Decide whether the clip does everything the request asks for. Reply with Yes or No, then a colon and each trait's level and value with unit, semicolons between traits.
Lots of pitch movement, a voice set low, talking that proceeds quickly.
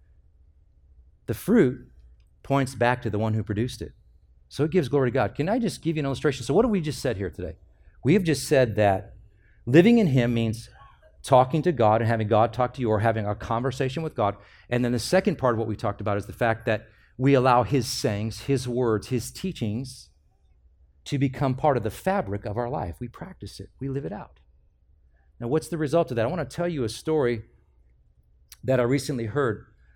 Yes: wide, 5.9 semitones; low, 115 Hz; fast, 220 wpm